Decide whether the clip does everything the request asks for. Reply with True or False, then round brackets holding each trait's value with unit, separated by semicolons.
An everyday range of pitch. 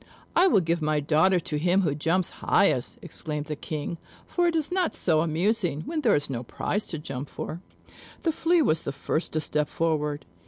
True (4.7 semitones)